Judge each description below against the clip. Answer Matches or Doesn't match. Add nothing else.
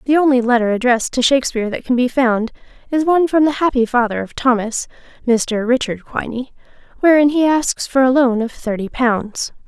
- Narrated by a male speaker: Doesn't match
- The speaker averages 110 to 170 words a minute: Doesn't match